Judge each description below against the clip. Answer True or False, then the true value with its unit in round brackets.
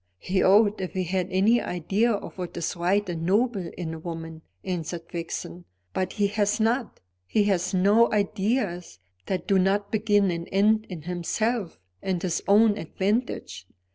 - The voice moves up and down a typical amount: True (3.1 semitones)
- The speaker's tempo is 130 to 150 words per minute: False (165 wpm)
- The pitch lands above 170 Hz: True (190 Hz)